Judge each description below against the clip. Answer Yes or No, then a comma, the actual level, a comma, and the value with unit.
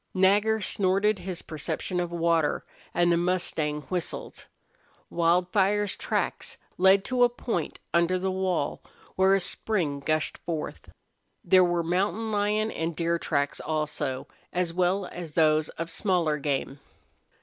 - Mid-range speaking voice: Yes, medium, 175 Hz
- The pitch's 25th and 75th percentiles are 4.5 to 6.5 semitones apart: No, average, 2.9 semitones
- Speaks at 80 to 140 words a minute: Yes, slow, 135 wpm